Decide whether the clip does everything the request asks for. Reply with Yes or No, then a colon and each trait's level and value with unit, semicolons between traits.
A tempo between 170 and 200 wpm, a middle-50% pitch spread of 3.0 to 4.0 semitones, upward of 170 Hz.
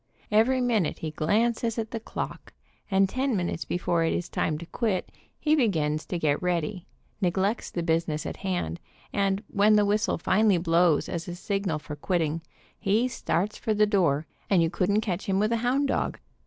No: average, 185 wpm; average, 4.4 semitones; high, 190 Hz